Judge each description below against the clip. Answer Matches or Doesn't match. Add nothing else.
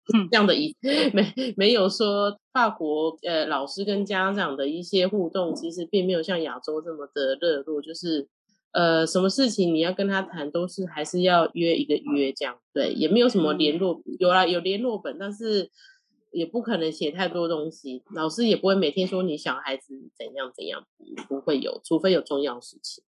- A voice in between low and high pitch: Matches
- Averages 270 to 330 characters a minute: Matches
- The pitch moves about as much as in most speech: Matches